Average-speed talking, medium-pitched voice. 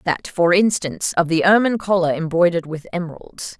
Yes: average, 165 wpm; medium, 175 Hz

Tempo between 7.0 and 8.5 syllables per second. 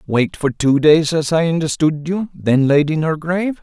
No: 5.0 syllables/s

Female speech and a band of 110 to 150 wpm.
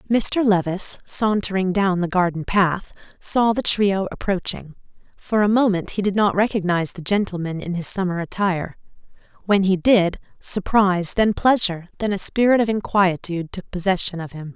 No: female; average, 160 wpm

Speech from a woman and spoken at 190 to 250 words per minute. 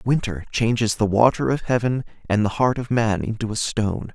No: male; fast, 205 wpm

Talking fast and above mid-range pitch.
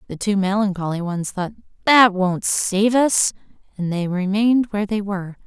No: average, 165 wpm; high, 200 Hz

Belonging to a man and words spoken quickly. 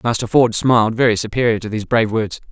Yes: male; fast, 215 wpm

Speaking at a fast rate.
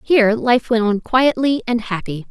No: average, 180 wpm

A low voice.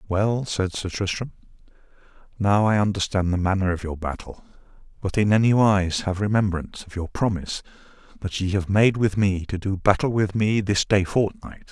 Yes: low, 100 Hz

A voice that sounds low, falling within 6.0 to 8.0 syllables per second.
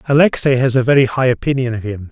Yes: low, 125 Hz; 6.7 syllables/s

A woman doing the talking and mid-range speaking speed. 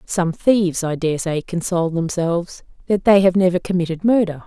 Yes: female; average, 175 wpm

